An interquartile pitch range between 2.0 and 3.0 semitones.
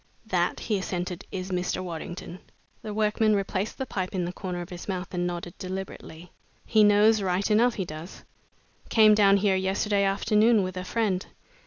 Yes: average, 2.7 semitones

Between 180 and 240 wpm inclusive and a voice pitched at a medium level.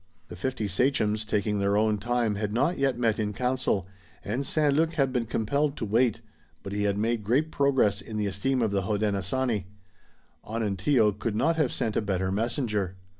No: average, 185 wpm; low, 110 Hz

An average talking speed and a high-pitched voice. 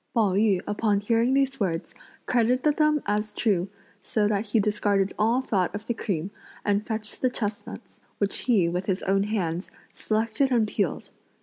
Yes: average, 170 wpm; high, 210 Hz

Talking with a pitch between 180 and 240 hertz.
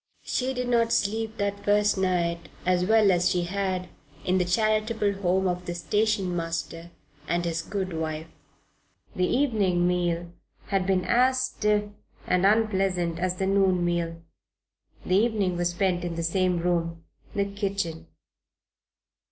Yes: medium, 185 Hz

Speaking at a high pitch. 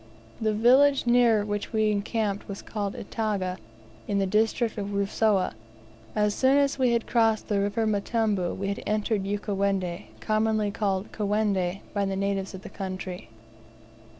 Yes: high, 205 Hz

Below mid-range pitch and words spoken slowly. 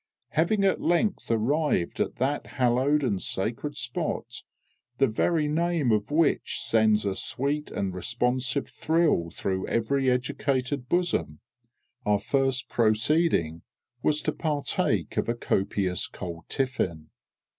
Yes: low, 125 Hz; slow, 125 wpm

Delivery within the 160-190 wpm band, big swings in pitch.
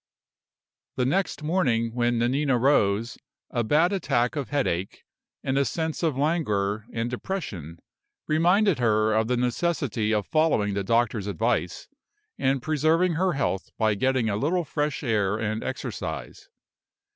No: average, 140 wpm; wide, 6.0 semitones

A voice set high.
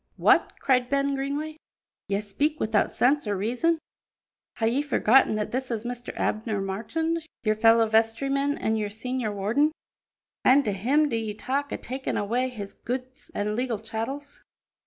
Yes: high, 245 Hz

